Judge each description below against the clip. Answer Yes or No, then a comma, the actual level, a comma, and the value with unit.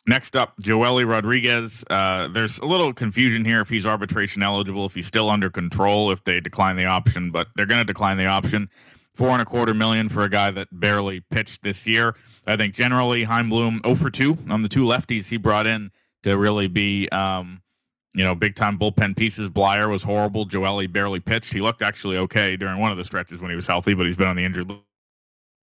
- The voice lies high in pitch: No, low, 105 Hz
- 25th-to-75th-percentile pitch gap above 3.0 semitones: No, average, 2.7 semitones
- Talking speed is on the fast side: Yes, fast, 220 wpm